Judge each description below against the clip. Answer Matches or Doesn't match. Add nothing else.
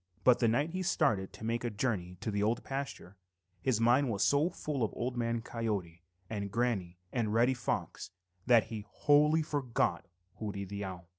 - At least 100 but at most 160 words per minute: Doesn't match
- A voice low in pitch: Matches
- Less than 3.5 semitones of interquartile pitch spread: Doesn't match